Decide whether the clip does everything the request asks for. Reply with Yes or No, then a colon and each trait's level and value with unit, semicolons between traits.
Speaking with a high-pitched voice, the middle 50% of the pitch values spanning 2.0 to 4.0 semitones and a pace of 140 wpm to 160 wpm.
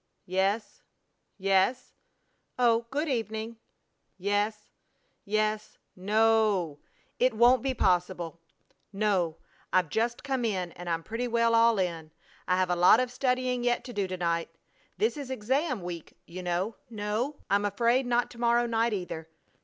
No: high, 215 Hz; average, 4.6 semitones; average, 155 wpm